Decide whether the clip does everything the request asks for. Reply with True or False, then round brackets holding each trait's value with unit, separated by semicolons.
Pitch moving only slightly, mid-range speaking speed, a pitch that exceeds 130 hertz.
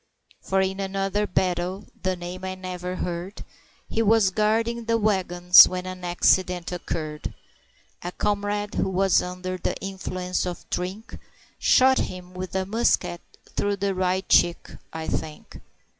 True (1.9 semitones; 145 wpm; 185 Hz)